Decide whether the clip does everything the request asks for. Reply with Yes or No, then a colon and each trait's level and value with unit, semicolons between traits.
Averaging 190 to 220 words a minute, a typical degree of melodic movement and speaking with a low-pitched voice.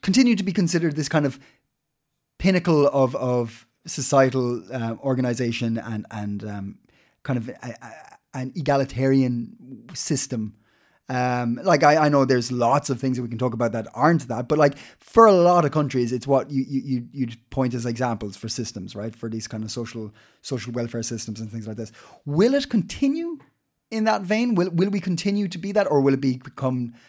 Yes: average, 195 wpm; average, 4.7 semitones; low, 130 Hz